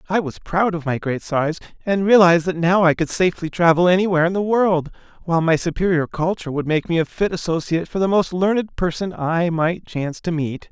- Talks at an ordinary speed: No, fast, 220 wpm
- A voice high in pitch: No, medium, 175 Hz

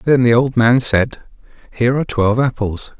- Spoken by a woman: No, male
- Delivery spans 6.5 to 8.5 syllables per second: No, 5.2 syllables/s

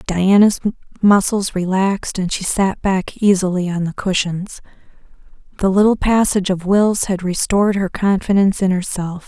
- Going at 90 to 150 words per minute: Yes, average, 140 wpm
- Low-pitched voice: No, high, 190 Hz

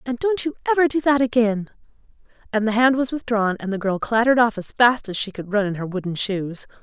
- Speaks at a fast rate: Yes, fast, 235 wpm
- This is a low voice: No, high, 225 Hz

